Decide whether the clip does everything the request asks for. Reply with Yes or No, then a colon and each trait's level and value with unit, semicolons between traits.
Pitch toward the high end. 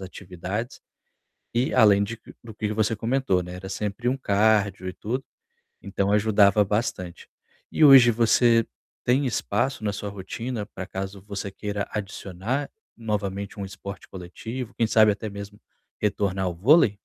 No: low, 105 Hz